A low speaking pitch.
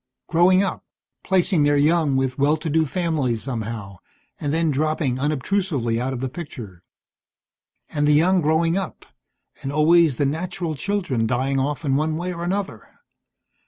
No: medium, 150 Hz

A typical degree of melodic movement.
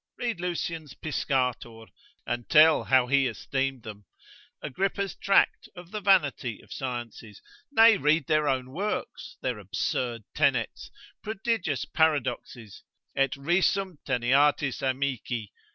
No: wide, 5.8 semitones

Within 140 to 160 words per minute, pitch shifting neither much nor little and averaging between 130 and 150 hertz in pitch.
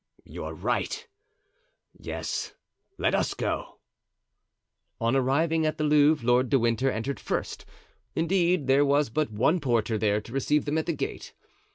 Yes: average, 150 wpm; average, 4.6 semitones; medium, 140 Hz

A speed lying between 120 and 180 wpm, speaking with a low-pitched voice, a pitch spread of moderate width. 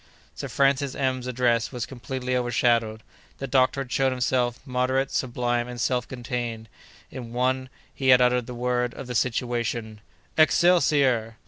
No: average, 145 wpm; low, 125 Hz; narrow, 1.4 semitones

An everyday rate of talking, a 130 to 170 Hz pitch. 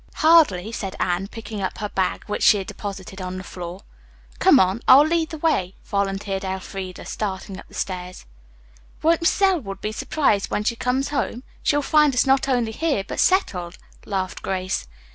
No: average, 180 wpm; high, 205 Hz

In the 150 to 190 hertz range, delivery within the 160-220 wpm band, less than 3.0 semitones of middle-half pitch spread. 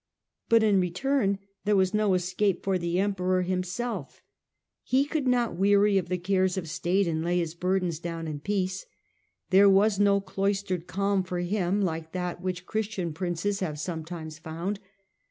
Yes: medium, 185 Hz; average, 165 wpm; narrow, 2.4 semitones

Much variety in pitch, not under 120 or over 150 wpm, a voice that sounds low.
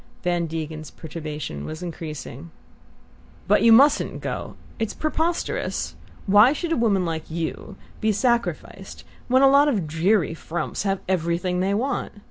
No: wide, 6.2 semitones; average, 140 wpm; medium, 185 Hz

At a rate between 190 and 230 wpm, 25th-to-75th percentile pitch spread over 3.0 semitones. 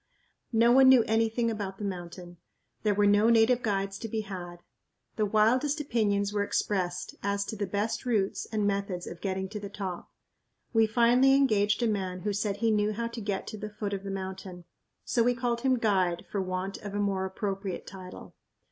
No: average, 200 wpm; average, 2.7 semitones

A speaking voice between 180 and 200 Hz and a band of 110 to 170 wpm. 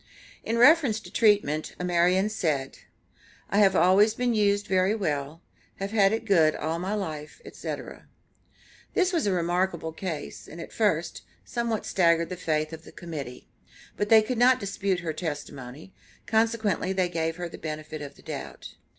Yes: medium, 185 Hz; average, 165 wpm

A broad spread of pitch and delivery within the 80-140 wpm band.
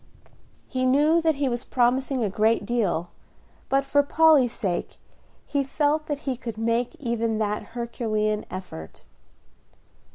No: average, 4.1 semitones; slow, 135 wpm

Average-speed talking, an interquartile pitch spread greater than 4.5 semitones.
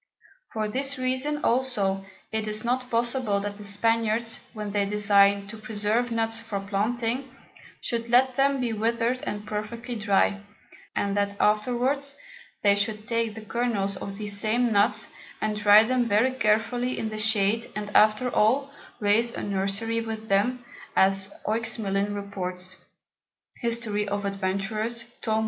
No: average, 145 wpm; narrow, 2.6 semitones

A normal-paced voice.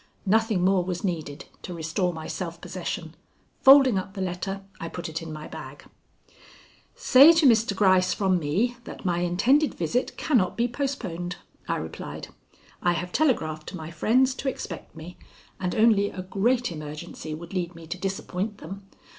Yes: average, 170 wpm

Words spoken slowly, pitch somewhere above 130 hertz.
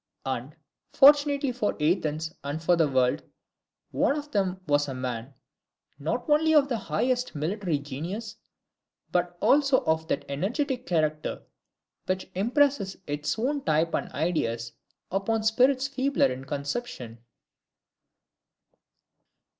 Yes: slow, 120 wpm; medium, 185 Hz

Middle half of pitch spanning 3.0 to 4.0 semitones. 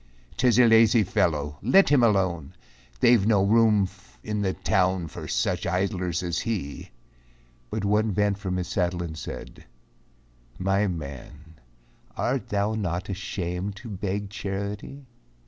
Yes: average, 3.3 semitones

